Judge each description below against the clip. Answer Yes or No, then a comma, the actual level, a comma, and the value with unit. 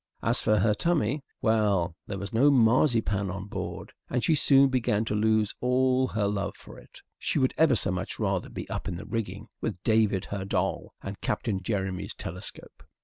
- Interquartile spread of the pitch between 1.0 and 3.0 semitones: No, average, 4.1 semitones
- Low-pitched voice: Yes, low, 110 Hz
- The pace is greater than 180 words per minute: Yes, average, 190 wpm